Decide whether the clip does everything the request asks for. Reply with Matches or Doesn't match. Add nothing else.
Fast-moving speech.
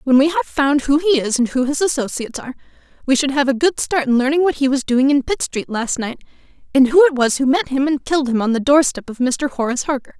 Matches